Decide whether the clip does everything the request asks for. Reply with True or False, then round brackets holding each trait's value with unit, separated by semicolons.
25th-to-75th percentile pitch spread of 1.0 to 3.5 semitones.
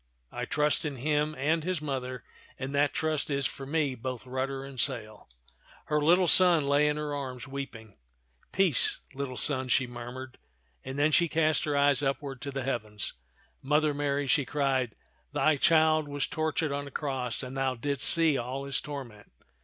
True (2.5 semitones)